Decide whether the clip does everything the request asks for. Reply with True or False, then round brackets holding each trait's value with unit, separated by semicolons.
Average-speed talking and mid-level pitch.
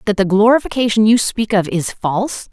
False (190 wpm; 205 Hz)